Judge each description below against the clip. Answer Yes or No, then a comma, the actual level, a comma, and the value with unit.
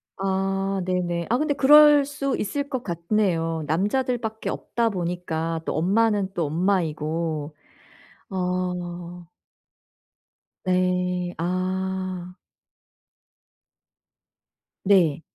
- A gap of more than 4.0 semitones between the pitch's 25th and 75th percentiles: No, average, 3.0 semitones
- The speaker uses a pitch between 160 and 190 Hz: Yes, medium, 185 Hz